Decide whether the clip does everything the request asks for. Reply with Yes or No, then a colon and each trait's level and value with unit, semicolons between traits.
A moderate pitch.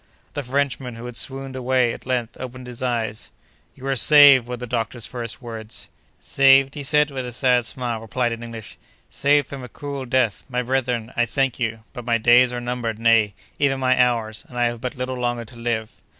No: low, 125 Hz